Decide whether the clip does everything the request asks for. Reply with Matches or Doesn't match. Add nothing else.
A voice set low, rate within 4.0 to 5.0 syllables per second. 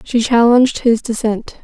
Doesn't match